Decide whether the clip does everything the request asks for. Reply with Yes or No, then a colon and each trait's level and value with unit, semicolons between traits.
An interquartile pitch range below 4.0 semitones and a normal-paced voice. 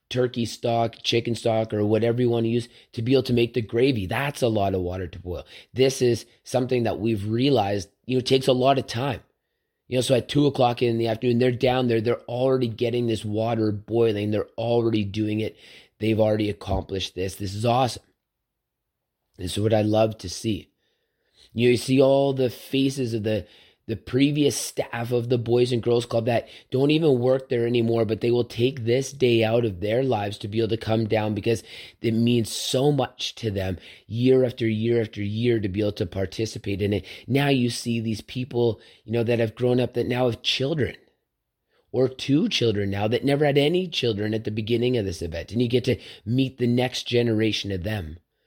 No: narrow, 2.6 semitones; fast, 215 wpm